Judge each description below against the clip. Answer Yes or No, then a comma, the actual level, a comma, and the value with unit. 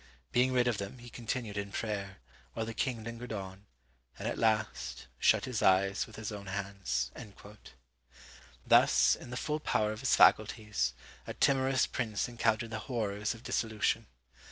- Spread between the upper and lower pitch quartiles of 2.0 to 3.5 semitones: Yes, average, 3.1 semitones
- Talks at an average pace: Yes, average, 160 wpm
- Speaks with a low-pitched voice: Yes, low, 110 Hz